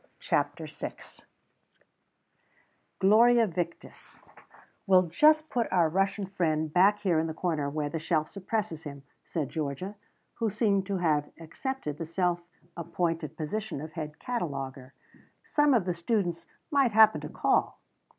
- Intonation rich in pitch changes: No, average, 4.9 semitones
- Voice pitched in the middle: Yes, medium, 175 Hz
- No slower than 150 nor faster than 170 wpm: No, average, 140 wpm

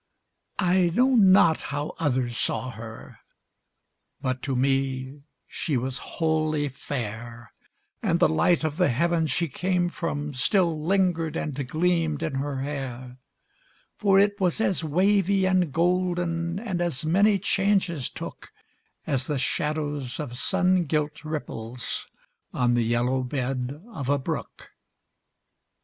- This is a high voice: No, medium, 150 Hz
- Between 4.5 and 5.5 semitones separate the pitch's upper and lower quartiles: Yes, average, 5.2 semitones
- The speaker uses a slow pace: Yes, slow, 130 wpm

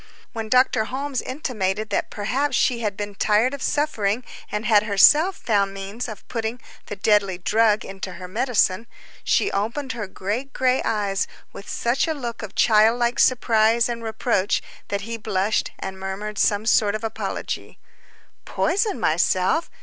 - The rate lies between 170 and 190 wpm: No, average, 155 wpm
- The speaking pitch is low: No, high, 220 Hz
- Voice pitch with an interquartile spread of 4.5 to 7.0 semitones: No, average, 3.4 semitones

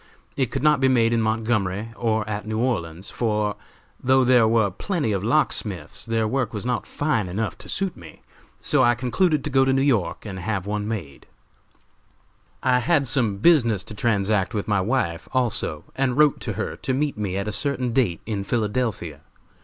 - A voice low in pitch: Yes, low, 115 Hz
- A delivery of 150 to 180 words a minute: No, average, 190 wpm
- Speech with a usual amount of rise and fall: Yes, average, 4.0 semitones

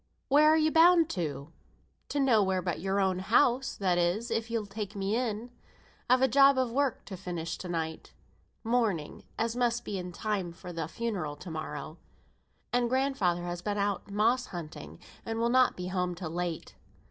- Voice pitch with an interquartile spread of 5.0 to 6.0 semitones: Yes, wide, 5.5 semitones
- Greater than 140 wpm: Yes, average, 180 wpm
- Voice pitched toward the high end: Yes, high, 200 Hz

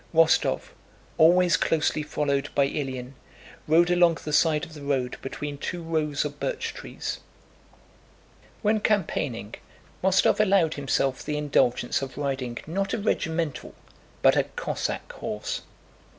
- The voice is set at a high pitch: No, medium, 150 Hz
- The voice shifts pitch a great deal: No, average, 3.5 semitones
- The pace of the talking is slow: Yes, slow, 130 wpm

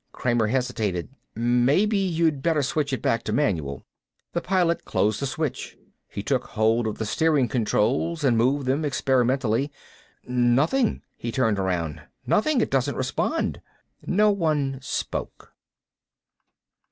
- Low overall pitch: Yes, low, 130 Hz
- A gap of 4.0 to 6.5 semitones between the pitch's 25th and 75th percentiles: Yes, wide, 5.6 semitones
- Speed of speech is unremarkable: No, slow, 130 wpm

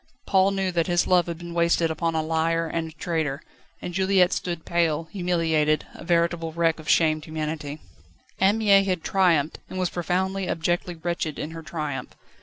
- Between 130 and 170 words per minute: No, average, 180 wpm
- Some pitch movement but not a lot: No, narrow, 2.0 semitones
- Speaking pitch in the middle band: Yes, medium, 170 Hz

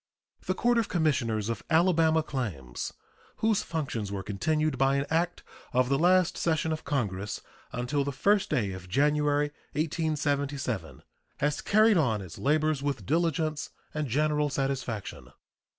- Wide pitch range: No, average, 4.2 semitones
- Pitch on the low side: No, medium, 145 Hz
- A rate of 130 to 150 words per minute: Yes, average, 140 wpm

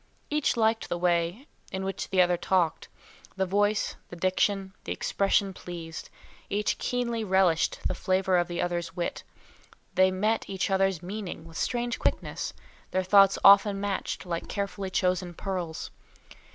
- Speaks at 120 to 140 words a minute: No, average, 150 wpm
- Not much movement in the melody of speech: Yes, narrow, 2.2 semitones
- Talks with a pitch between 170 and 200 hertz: Yes, high, 190 Hz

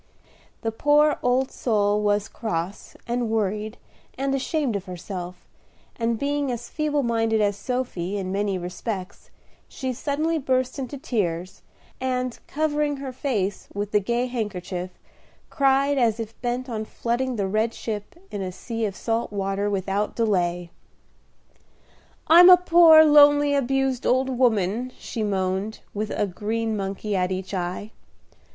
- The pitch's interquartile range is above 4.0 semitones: Yes, average, 4.7 semitones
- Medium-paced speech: Yes, average, 145 wpm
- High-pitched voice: Yes, high, 225 Hz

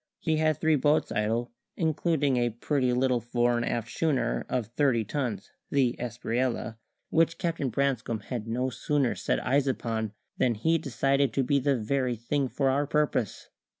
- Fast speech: No, average, 165 wpm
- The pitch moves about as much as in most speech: Yes, average, 3.3 semitones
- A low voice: Yes, low, 130 Hz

